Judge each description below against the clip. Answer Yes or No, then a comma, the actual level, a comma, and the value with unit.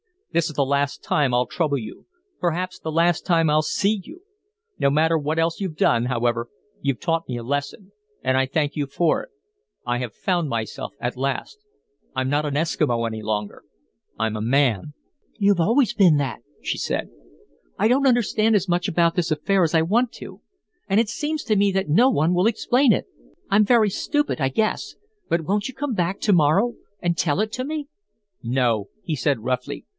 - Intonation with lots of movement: Yes, wide, 6.8 semitones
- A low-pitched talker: No, medium, 165 Hz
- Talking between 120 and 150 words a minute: No, average, 195 wpm